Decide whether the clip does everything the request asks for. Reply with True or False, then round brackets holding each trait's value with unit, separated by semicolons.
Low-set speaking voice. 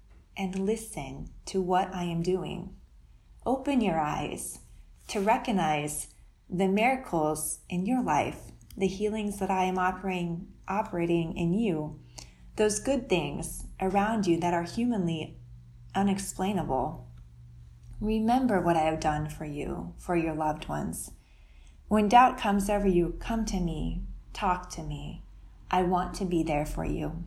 False (175 Hz)